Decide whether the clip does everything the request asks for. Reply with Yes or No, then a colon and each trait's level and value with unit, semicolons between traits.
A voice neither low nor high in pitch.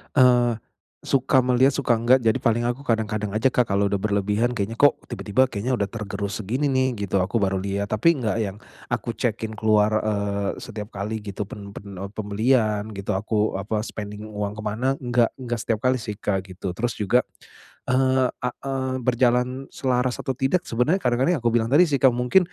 No: low, 115 Hz